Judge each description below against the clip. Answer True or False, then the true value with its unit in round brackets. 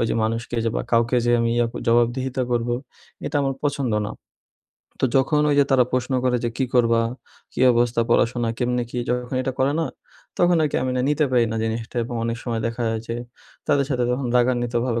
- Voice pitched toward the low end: True (120 Hz)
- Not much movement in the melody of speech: True (1.9 semitones)